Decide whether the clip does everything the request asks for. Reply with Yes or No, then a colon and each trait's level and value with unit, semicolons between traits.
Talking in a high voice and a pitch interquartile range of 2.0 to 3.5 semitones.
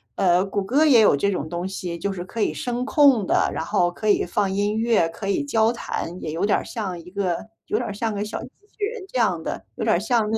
No: high, 205 Hz; average, 4.3 semitones